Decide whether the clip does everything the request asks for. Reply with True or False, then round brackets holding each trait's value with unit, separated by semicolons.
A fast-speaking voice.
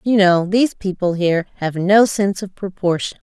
False (180 wpm)